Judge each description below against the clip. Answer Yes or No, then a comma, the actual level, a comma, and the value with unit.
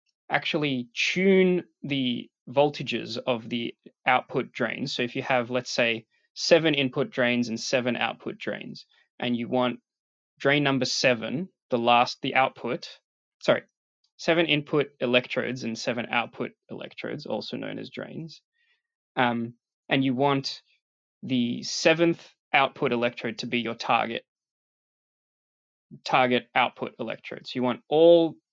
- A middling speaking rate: No, slow, 130 wpm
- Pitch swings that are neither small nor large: Yes, average, 3.5 semitones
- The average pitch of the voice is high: No, low, 130 Hz